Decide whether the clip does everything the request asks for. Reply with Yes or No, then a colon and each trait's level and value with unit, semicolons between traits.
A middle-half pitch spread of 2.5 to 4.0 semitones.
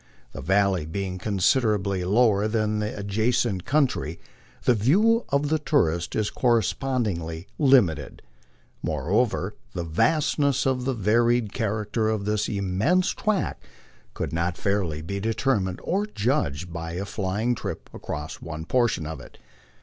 No: wide, 5.5 semitones